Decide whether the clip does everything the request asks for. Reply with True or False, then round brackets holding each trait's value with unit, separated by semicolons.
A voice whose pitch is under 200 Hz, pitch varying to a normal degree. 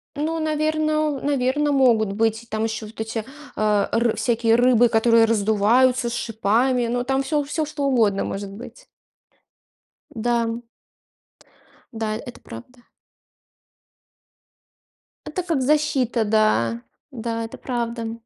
False (235 Hz; 3.4 semitones)